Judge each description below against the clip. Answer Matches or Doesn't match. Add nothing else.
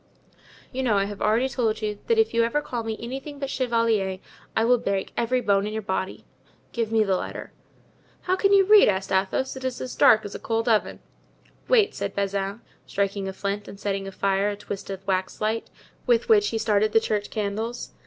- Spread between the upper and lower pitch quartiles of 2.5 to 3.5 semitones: Doesn't match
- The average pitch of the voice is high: Matches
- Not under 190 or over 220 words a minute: Matches